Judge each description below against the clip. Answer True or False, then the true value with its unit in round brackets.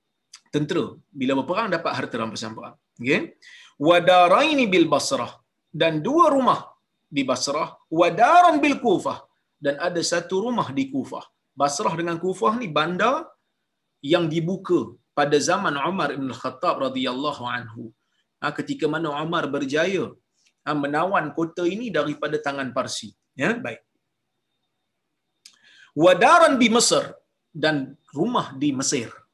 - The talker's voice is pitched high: False (165 Hz)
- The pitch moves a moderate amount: True (4.9 semitones)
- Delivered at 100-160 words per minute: True (125 wpm)